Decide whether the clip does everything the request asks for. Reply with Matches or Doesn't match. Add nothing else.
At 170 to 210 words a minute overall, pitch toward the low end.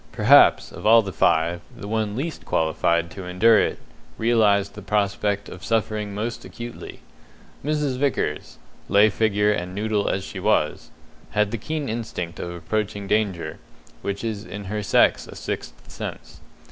Doesn't match